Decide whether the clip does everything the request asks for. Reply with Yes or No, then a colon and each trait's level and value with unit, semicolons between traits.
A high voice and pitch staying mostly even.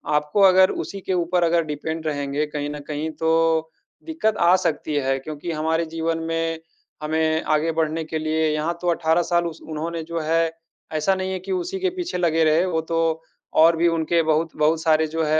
No: medium, 160 Hz; narrow, 1.6 semitones